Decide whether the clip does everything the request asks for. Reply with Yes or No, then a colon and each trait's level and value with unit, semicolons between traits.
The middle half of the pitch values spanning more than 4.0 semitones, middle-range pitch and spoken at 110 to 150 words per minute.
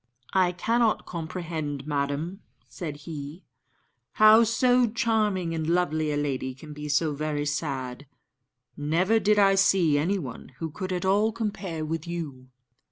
Yes: average, 4.9 semitones; medium, 165 Hz; average, 140 wpm